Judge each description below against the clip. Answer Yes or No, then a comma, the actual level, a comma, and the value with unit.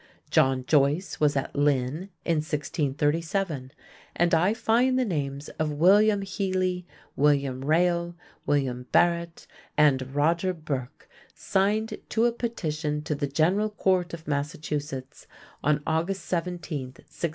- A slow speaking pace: Yes, slow, 125 wpm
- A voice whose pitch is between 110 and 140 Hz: No, medium, 160 Hz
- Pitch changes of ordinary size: Yes, average, 4.2 semitones